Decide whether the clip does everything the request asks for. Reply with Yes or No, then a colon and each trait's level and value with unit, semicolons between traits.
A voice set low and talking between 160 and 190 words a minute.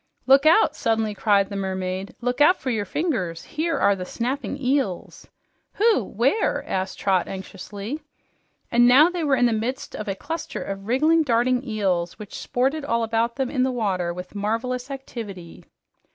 No: high, 235 Hz; average, 170 wpm